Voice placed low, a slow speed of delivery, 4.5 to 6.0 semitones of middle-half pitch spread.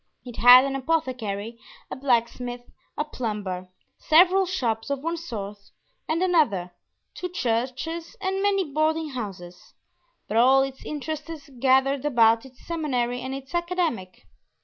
No: very high, 265 Hz; slow, 130 wpm; wide, 5.6 semitones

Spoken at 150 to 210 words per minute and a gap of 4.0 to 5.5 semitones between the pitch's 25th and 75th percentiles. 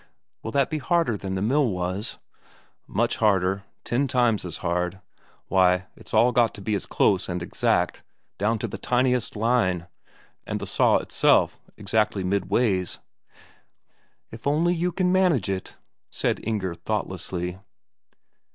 No: average, 140 wpm; average, 5.0 semitones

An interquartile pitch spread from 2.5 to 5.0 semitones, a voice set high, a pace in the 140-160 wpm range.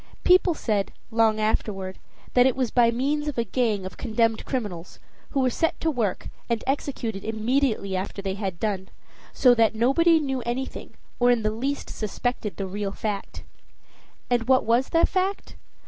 No: average, 4.0 semitones; high, 230 Hz; average, 170 wpm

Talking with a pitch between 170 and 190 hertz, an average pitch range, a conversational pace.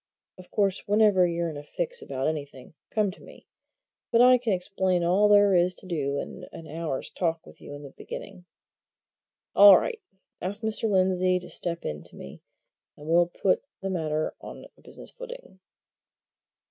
Yes: medium, 185 Hz; average, 4.0 semitones; average, 175 wpm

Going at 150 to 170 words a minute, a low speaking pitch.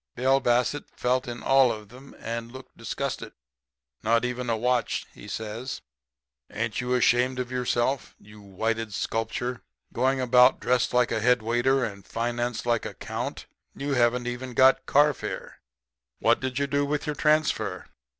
Yes: average, 160 wpm; low, 125 Hz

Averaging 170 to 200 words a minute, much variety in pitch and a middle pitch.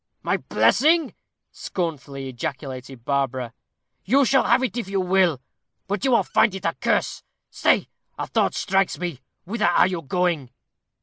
No: average, 150 wpm; wide, 7.2 semitones; medium, 180 Hz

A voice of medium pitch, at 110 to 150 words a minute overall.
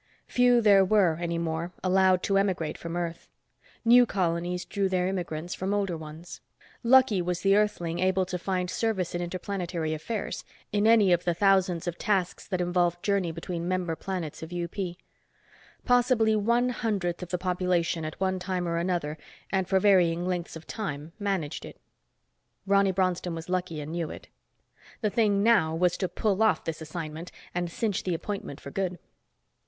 No: medium, 180 Hz; average, 170 wpm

